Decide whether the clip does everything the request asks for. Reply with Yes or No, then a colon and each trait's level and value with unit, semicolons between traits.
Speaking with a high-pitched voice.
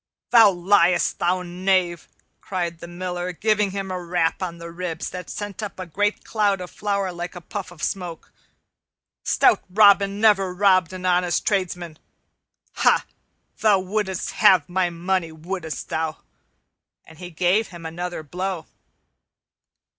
No: medium, 180 Hz